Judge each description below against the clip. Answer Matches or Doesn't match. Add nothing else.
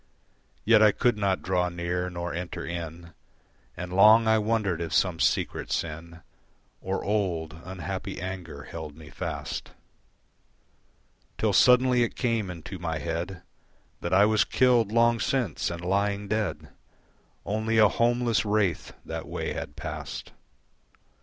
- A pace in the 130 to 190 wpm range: Matches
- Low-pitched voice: Matches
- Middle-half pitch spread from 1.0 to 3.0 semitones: Doesn't match